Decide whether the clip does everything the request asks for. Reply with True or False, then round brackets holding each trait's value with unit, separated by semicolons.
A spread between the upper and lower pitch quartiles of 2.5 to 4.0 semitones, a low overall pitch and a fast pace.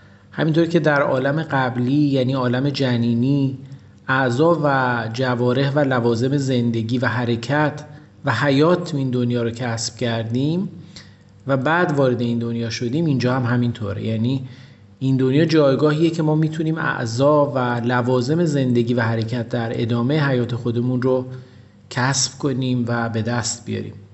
False (3.0 semitones; 130 Hz; 140 wpm)